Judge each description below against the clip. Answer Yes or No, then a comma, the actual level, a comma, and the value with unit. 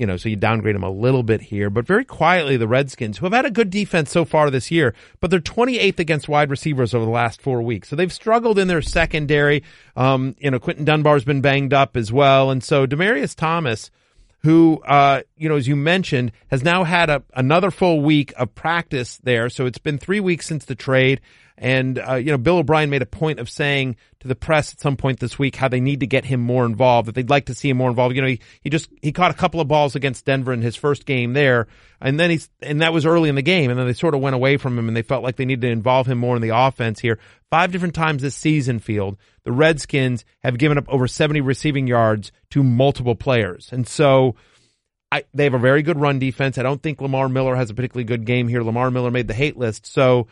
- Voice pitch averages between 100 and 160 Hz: Yes, low, 135 Hz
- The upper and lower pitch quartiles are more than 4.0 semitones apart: No, average, 3.7 semitones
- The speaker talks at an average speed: No, fast, 255 wpm